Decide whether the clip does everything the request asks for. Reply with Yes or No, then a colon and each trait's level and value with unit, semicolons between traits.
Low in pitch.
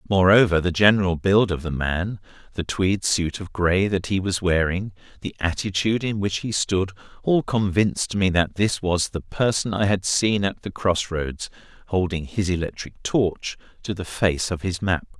Yes: very low, 95 Hz